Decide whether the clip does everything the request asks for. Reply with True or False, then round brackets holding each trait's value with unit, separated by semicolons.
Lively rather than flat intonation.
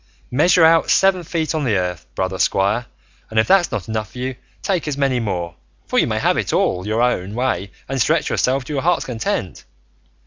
True (7.4 semitones)